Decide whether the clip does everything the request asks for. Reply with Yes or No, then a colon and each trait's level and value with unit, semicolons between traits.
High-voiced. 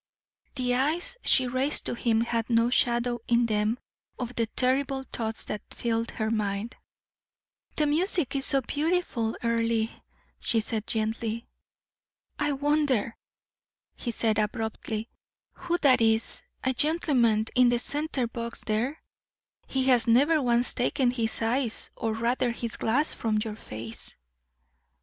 Yes: high, 235 Hz